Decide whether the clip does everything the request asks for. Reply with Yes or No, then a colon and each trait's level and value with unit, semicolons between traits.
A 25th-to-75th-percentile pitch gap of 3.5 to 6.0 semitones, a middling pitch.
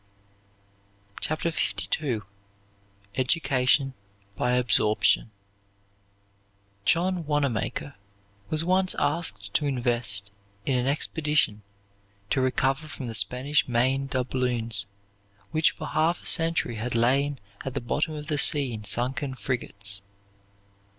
No: average, 4.0 semitones; low, 130 Hz